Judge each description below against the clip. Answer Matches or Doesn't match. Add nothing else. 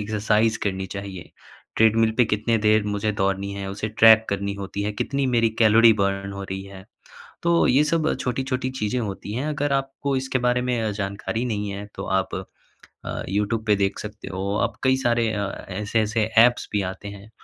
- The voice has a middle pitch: Doesn't match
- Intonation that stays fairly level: Doesn't match